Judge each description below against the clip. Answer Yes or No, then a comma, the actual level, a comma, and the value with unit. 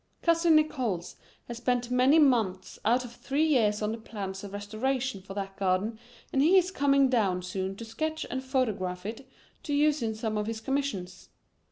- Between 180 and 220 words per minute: Yes, average, 185 wpm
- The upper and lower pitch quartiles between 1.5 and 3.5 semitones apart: No, average, 5.3 semitones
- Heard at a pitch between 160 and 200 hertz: No, high, 235 Hz